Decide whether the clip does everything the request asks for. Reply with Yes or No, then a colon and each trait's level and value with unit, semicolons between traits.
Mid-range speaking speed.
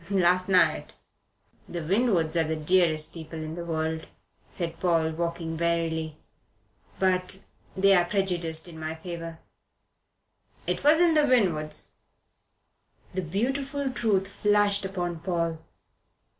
No: slow, 115 wpm